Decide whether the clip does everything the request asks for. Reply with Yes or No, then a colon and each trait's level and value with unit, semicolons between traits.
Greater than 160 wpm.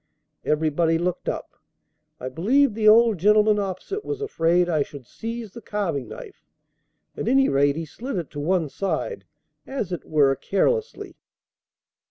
No: average, 150 wpm